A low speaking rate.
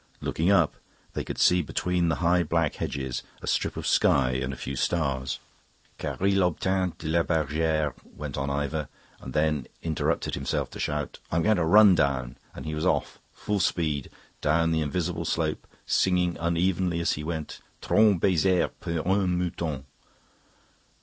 No: average, 165 wpm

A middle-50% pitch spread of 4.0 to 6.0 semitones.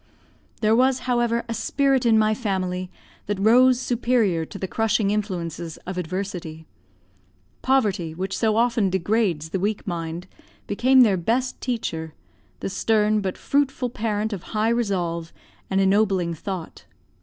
Yes: average, 4.3 semitones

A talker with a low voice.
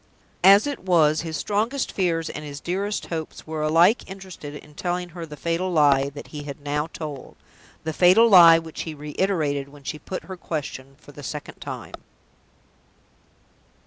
No: medium, 160 Hz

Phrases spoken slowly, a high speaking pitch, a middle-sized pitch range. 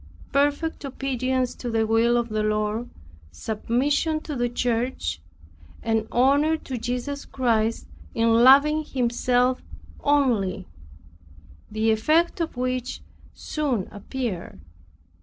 Yes: slow, 105 wpm; high, 245 Hz; average, 3.6 semitones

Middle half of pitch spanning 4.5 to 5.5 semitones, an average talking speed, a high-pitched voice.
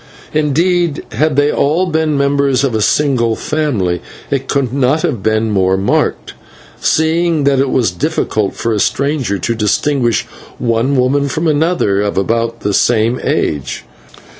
No: average, 5.2 semitones; average, 150 wpm; low, 135 Hz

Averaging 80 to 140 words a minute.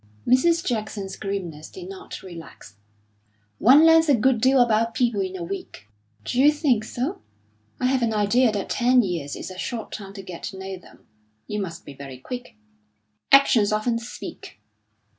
No: average, 170 wpm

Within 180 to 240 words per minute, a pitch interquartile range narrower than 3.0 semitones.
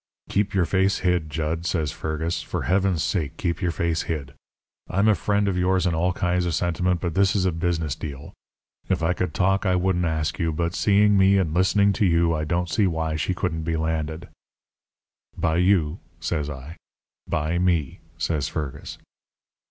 Yes: average, 185 wpm; narrow, 2.6 semitones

